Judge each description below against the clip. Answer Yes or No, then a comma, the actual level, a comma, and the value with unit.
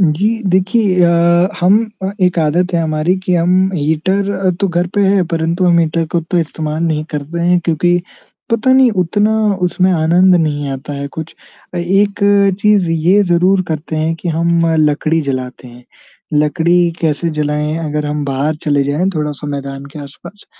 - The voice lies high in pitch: No, medium, 170 Hz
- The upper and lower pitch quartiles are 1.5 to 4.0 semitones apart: Yes, average, 3.3 semitones